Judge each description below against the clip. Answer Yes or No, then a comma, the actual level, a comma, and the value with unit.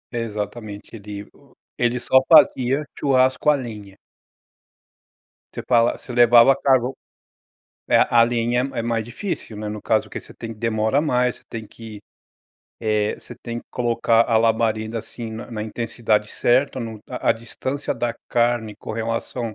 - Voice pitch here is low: Yes, low, 115 Hz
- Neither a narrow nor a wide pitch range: No, narrow, 1.9 semitones